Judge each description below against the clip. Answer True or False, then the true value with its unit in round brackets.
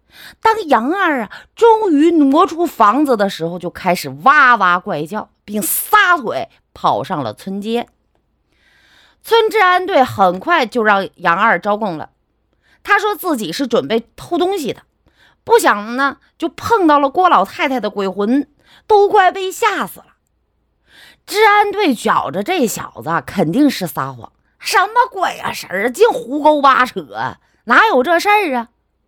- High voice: True (285 Hz)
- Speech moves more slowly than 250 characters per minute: True (210 characters per minute)